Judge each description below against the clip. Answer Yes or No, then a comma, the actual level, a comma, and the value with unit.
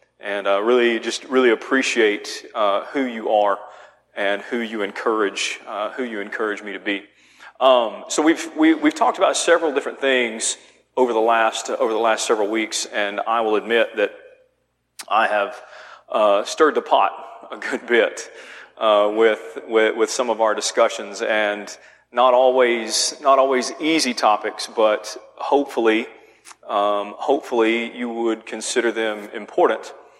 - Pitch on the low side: Yes, low, 115 Hz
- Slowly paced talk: No, average, 155 wpm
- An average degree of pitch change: Yes, average, 3.7 semitones